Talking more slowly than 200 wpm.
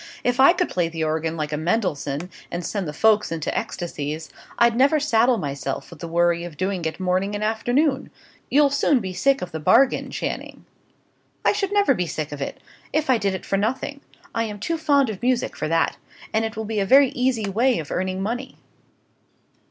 No: fast, 205 wpm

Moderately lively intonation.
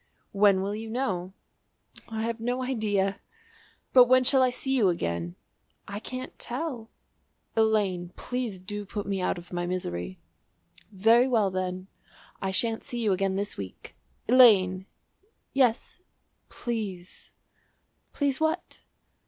Yes: average, 4.7 semitones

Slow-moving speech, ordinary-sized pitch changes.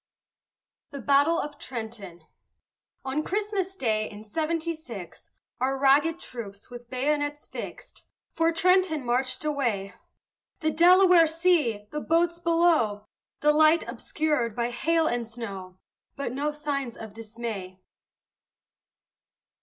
No: slow, 115 wpm; wide, 6.0 semitones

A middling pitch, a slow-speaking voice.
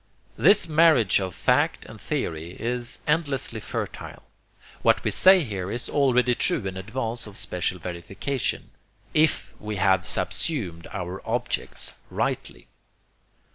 No: low, 110 Hz; slow, 125 wpm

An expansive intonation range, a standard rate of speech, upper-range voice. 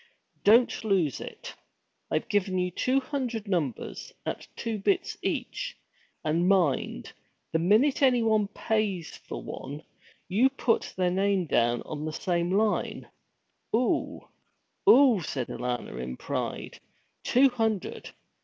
No: wide, 5.8 semitones; slow, 125 wpm; high, 195 Hz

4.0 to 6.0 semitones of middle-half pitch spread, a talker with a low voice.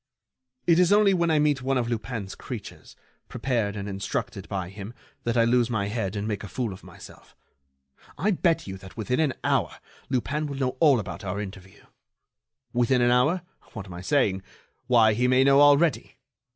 Yes: wide, 5.6 semitones; low, 120 Hz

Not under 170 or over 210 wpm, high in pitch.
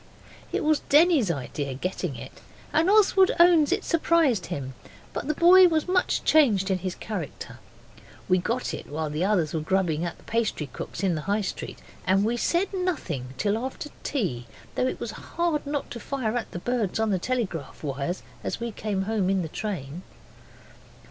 Yes: average, 185 wpm; high, 210 Hz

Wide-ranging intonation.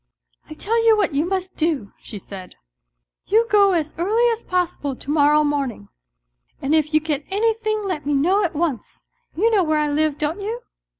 Yes: wide, 5.7 semitones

